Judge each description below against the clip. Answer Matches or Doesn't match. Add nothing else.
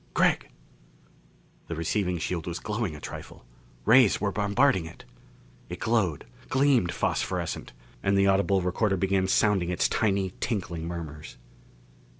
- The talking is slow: Matches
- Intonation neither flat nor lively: Matches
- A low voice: Matches